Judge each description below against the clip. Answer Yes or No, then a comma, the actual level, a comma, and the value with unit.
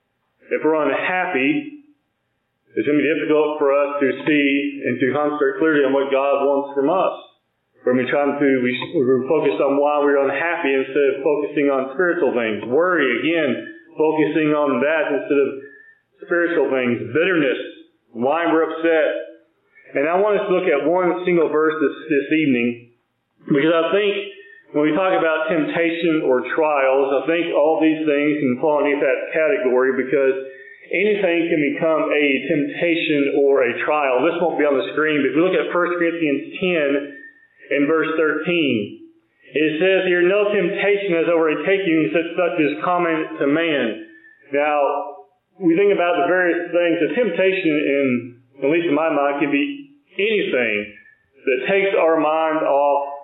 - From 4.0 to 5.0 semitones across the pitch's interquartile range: Yes, average, 4.4 semitones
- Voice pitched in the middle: Yes, medium, 160 Hz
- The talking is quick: No, average, 170 wpm